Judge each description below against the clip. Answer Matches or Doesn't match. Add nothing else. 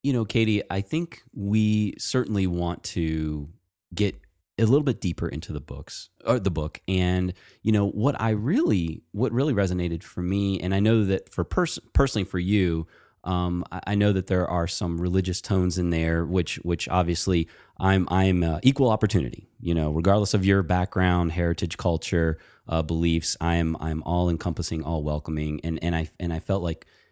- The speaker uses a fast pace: Doesn't match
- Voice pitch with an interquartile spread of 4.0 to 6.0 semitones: Doesn't match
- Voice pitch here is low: Matches